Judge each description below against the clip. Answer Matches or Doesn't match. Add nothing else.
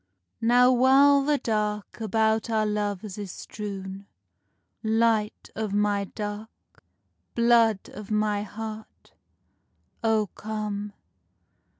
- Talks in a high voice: Matches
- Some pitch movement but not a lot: Doesn't match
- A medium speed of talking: Doesn't match